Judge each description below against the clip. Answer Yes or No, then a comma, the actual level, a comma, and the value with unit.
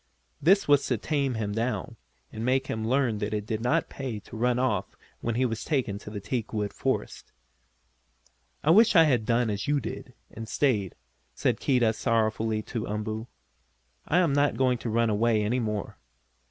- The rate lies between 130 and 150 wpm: No, average, 180 wpm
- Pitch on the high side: No, low, 115 Hz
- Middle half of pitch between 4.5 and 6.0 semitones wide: No, average, 3.4 semitones